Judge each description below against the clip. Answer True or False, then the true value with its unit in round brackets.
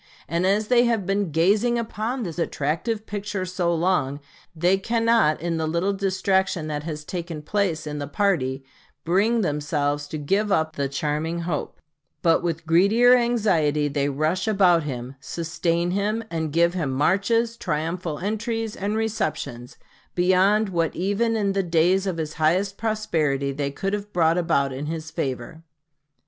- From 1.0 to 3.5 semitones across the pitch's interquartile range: False (4.8 semitones)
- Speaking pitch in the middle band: True (175 Hz)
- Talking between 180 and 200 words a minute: False (160 wpm)